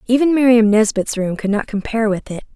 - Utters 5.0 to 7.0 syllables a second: Yes, 6.0 syllables/s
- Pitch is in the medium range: No, high, 225 Hz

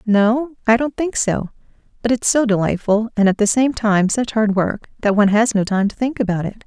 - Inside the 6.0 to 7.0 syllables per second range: No, 5.2 syllables/s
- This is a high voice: Yes, high, 220 Hz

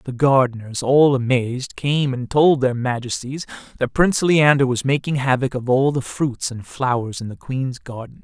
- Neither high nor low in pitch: No, low, 130 Hz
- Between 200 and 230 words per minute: No, average, 180 wpm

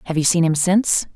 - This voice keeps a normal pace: No, fast, 260 wpm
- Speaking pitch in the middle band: Yes, medium, 170 Hz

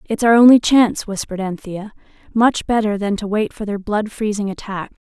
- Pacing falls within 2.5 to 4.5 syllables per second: No, 5.4 syllables/s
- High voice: Yes, high, 210 Hz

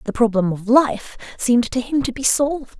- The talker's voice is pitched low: No, high, 245 Hz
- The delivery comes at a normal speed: No, fast, 215 wpm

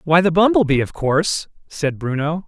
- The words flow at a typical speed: Yes, average, 195 wpm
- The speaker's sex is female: No, male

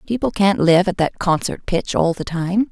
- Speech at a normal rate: No, fast, 220 wpm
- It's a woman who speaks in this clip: Yes, female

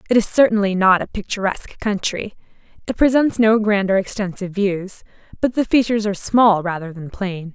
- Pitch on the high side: Yes, high, 205 Hz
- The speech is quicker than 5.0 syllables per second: Yes, 5.6 syllables/s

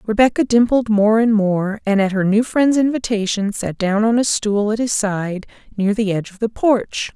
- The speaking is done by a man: No, female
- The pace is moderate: No, fast, 210 wpm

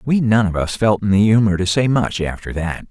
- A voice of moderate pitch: No, low, 105 Hz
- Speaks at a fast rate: Yes, fast, 270 wpm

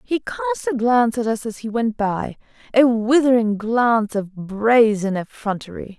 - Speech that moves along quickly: No, average, 160 wpm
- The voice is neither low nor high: No, high, 235 Hz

